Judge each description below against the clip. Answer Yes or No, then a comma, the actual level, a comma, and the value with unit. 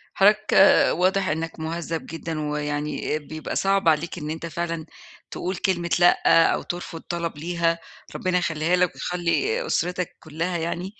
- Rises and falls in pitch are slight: Yes, narrow, 2.2 semitones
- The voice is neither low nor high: Yes, medium, 170 Hz